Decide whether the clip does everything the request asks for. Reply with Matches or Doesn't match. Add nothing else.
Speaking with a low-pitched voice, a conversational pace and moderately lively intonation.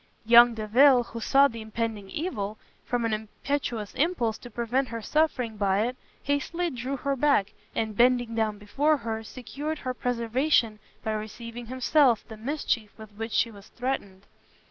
Doesn't match